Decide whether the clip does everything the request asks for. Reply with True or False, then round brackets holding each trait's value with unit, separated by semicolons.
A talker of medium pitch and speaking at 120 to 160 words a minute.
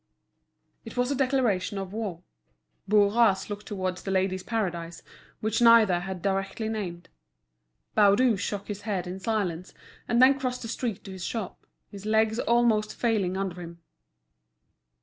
False (205 Hz; 150 wpm)